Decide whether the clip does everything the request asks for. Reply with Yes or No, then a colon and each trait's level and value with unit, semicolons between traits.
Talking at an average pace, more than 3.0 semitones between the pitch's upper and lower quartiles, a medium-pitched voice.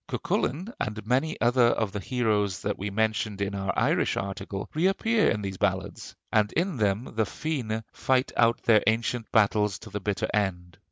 No: average, 175 wpm; average, 3.6 semitones; low, 110 Hz